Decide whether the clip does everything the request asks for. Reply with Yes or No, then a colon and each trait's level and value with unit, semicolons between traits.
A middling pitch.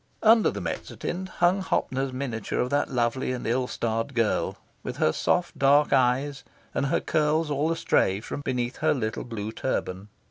No: low, 130 Hz